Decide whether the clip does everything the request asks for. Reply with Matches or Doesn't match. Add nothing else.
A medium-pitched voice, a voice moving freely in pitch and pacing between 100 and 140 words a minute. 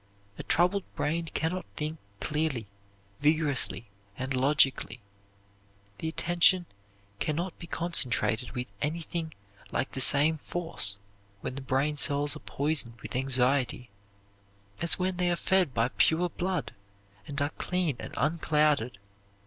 Doesn't match